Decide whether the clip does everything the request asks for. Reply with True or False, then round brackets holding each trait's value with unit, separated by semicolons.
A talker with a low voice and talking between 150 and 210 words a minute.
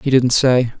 False (125 Hz; 225 wpm)